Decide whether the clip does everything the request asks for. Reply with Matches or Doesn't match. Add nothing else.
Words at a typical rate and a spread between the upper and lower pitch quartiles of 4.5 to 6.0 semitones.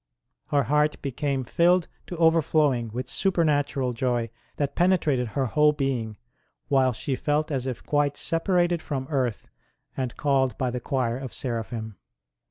Doesn't match